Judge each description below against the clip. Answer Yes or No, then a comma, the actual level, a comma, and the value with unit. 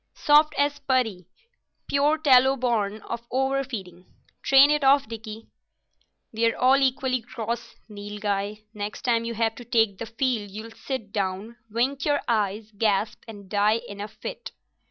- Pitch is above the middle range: Yes, high, 230 Hz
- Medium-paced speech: Yes, average, 150 wpm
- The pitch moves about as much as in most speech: Yes, average, 4.2 semitones